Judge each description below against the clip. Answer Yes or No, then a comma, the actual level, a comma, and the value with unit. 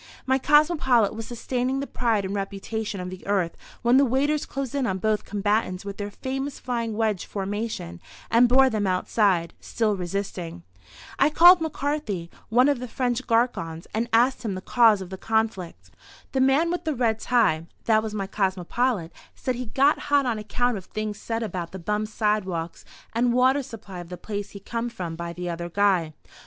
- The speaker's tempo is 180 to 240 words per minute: Yes, average, 190 wpm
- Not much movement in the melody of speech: No, average, 4.7 semitones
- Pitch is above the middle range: Yes, high, 220 Hz